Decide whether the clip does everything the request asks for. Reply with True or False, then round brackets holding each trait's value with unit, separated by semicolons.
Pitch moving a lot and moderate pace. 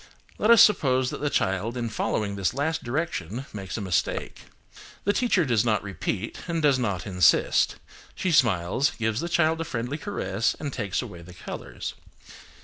True (7.8 semitones; 170 wpm)